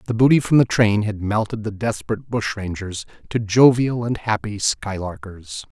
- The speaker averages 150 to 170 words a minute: Yes, average, 155 wpm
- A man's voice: Yes, male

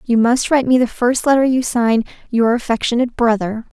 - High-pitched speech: Yes, high, 240 Hz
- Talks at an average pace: Yes, average, 190 wpm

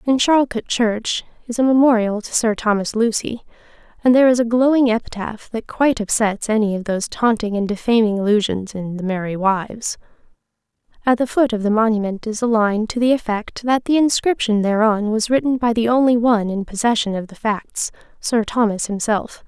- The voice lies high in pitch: Yes, high, 225 Hz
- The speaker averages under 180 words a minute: No, average, 185 wpm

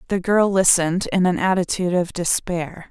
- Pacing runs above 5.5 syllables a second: No, 5.2 syllables/s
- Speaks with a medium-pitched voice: Yes, medium, 180 Hz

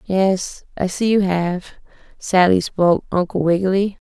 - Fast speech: No, slow, 135 wpm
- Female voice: Yes, female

